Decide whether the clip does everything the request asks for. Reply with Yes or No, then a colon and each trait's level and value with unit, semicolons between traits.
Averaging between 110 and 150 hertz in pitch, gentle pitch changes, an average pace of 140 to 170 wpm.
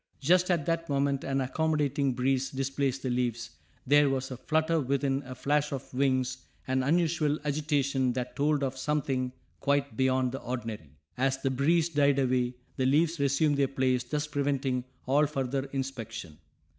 Yes: low, 135 Hz; narrow, 2.1 semitones; average, 160 wpm